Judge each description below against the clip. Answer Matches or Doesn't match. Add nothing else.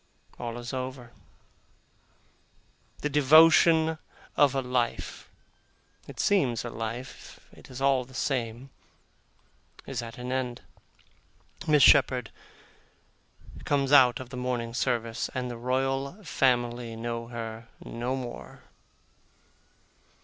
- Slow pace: Matches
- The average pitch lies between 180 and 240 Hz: Doesn't match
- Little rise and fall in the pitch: Matches